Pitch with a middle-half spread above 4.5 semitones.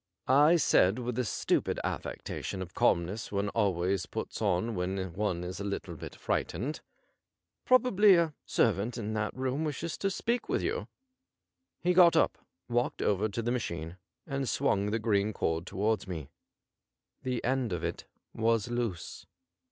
Yes: average, 5.3 semitones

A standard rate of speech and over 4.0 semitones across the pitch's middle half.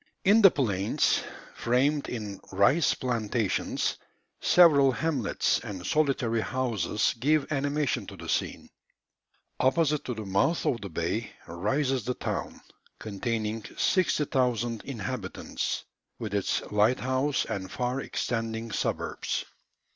No: slow, 110 wpm; average, 4.7 semitones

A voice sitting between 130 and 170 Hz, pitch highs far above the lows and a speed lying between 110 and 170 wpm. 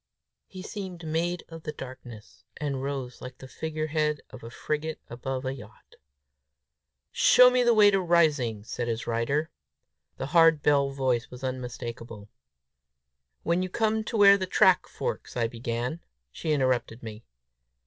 Yes: medium, 140 Hz; wide, 5.7 semitones; average, 150 wpm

